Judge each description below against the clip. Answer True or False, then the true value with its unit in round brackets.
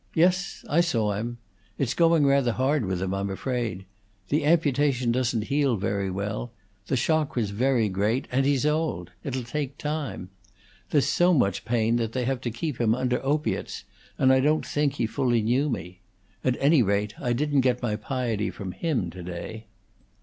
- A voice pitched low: True (125 Hz)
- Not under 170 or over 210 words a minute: True (180 wpm)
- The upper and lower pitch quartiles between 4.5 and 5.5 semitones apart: True (4.9 semitones)